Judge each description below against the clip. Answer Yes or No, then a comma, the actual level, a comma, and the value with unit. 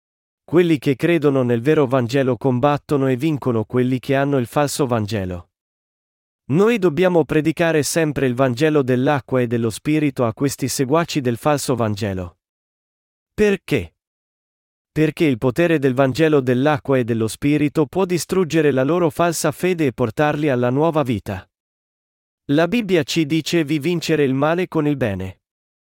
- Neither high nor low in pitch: Yes, medium, 145 Hz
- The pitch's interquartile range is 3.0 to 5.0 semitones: Yes, average, 4.3 semitones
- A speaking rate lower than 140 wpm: No, average, 150 wpm